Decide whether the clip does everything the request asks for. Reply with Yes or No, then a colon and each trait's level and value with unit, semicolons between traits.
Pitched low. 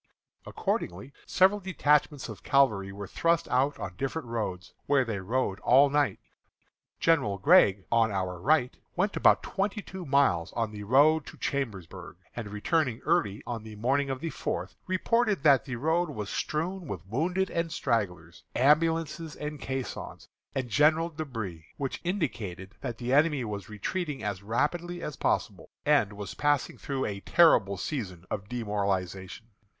Yes: low, 130 Hz